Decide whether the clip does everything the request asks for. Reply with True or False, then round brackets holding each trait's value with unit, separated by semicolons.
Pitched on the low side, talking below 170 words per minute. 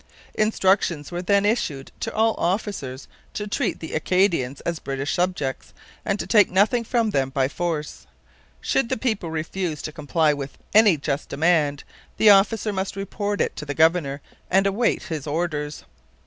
False (175 Hz; 160 wpm)